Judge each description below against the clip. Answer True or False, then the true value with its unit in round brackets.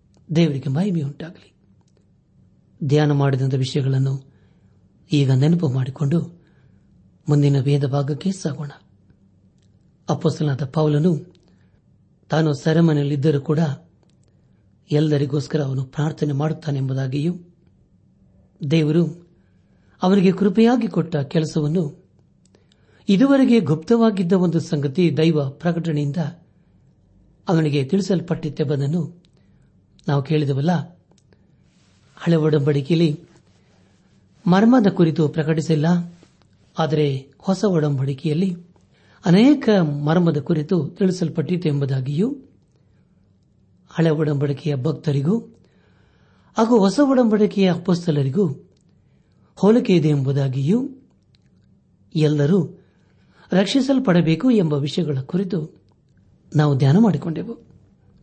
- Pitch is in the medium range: True (160 Hz)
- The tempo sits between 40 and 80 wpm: True (70 wpm)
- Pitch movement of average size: True (3.7 semitones)